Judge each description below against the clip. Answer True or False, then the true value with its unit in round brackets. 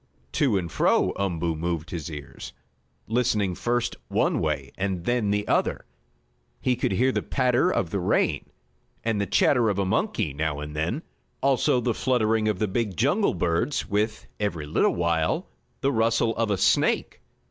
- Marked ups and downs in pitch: True (5.9 semitones)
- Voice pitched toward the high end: False (105 Hz)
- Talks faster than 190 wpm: False (170 wpm)